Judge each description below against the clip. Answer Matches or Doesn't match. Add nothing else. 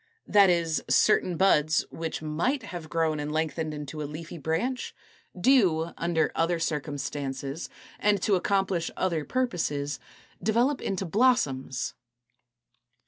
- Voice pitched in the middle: Matches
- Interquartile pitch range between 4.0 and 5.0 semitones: Matches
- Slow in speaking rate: Matches